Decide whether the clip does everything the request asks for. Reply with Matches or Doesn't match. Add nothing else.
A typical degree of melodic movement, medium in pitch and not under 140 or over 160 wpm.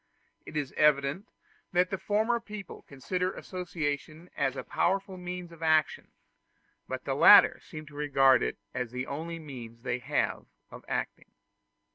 Matches